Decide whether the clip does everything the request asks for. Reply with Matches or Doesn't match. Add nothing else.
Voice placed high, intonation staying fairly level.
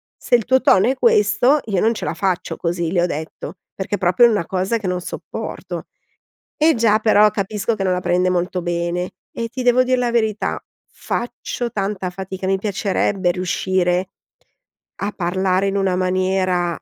Doesn't match